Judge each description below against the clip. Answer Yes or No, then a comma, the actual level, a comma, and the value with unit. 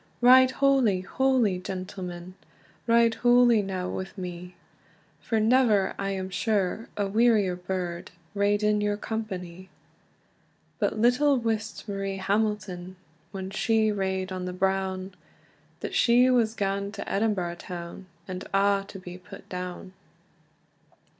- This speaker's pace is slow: Yes, slow, 125 wpm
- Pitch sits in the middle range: No, high, 195 Hz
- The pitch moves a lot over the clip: No, average, 3.1 semitones